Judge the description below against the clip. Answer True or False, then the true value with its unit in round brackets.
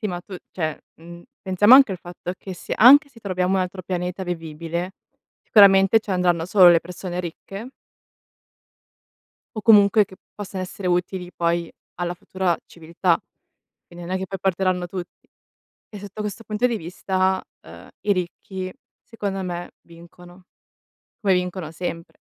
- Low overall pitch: False (185 Hz)